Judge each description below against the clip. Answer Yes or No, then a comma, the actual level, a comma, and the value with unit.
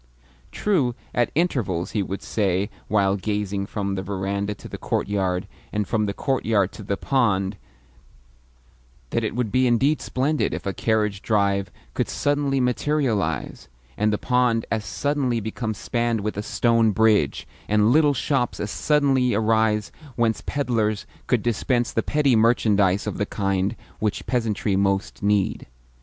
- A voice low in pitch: Yes, low, 110 Hz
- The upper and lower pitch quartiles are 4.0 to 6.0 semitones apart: No, average, 3.6 semitones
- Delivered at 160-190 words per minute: No, average, 150 wpm